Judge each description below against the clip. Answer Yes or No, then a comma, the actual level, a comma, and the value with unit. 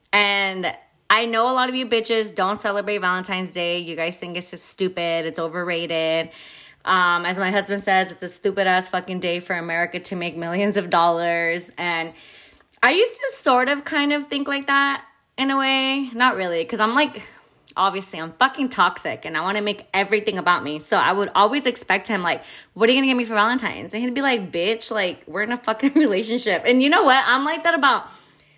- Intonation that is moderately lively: No, wide, 6.0 semitones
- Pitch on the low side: No, high, 200 Hz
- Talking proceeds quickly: Yes, fast, 215 wpm